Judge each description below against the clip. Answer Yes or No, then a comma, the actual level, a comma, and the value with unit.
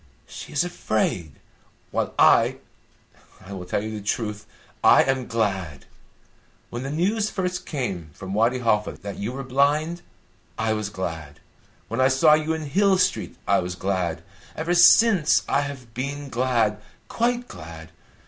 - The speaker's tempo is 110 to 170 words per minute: Yes, average, 155 wpm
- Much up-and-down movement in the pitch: Yes, wide, 7.2 semitones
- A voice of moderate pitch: No, low, 125 Hz